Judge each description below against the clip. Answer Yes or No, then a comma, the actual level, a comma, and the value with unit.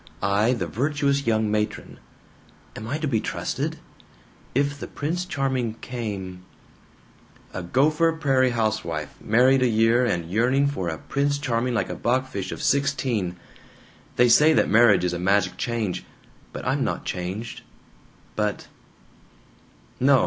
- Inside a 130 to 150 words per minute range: Yes, average, 140 wpm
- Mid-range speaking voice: No, low, 120 Hz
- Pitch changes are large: No, average, 4.8 semitones